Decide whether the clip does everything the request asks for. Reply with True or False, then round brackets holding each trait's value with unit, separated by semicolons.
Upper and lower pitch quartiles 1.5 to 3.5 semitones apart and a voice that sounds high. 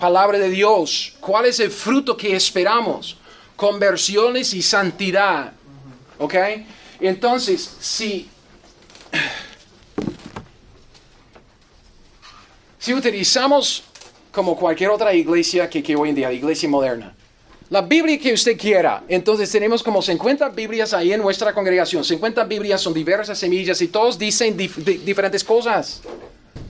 False (4.1 semitones; 200 Hz)